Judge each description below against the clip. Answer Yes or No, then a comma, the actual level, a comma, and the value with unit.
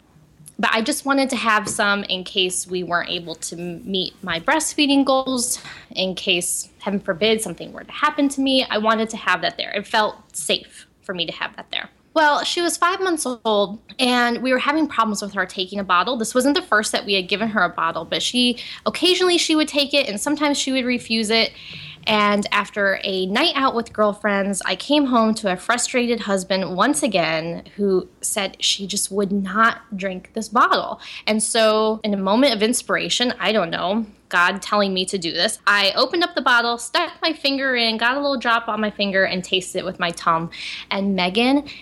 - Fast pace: Yes, fast, 210 wpm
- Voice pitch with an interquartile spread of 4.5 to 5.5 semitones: Yes, average, 4.8 semitones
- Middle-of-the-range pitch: No, high, 215 Hz